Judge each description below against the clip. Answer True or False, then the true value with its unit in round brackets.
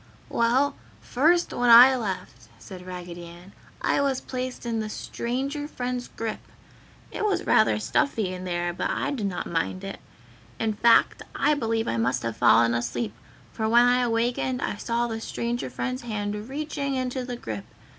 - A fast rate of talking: False (170 wpm)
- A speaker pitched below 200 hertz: False (230 Hz)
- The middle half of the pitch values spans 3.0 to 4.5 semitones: False (5.6 semitones)